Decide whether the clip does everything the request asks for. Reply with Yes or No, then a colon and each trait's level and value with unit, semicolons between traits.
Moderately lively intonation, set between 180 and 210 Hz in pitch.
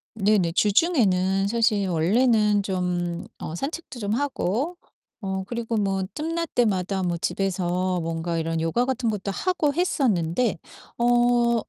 Yes: average, 5.0 semitones; high, 205 Hz